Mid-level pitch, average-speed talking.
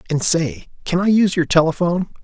Yes: medium, 165 Hz; average, 190 wpm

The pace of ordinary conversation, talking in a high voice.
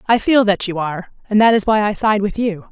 No: fast, 285 wpm; high, 210 Hz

